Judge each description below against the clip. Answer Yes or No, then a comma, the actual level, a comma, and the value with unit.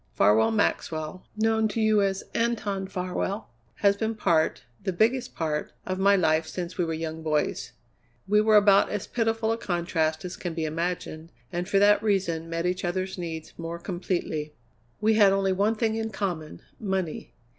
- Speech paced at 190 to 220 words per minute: No, average, 175 wpm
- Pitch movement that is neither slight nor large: Yes, average, 4.1 semitones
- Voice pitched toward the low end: No, medium, 185 Hz